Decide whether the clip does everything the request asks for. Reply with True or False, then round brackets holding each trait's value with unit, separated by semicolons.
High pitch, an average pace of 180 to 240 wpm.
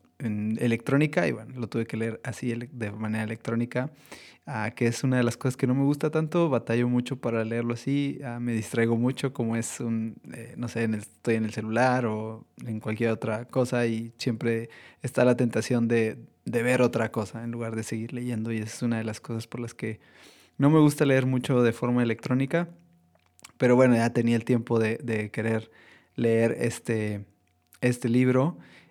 False (115 Hz; 185 wpm)